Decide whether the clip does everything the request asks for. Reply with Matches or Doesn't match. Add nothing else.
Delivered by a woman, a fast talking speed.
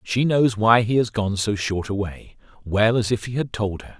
Doesn't match